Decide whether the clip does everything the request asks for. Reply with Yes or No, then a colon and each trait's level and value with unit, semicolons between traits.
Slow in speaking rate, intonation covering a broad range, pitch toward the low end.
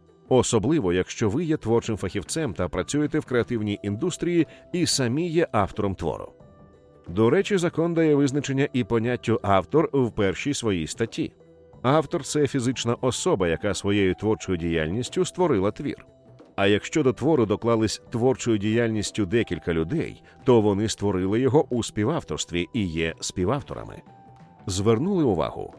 No: average, 135 wpm; wide, 5.7 semitones; low, 115 Hz